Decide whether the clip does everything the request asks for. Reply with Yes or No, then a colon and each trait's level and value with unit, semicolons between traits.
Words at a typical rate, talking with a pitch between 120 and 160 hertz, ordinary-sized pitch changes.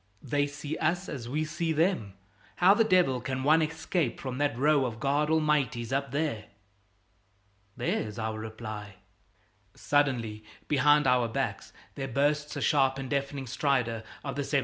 Yes: average, 155 wpm; medium, 140 Hz; average, 3.8 semitones